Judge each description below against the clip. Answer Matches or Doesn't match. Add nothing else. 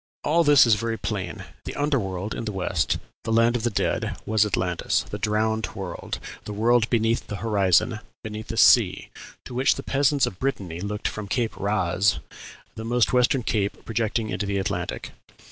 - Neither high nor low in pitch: Doesn't match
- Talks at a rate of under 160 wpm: Doesn't match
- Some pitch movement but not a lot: Matches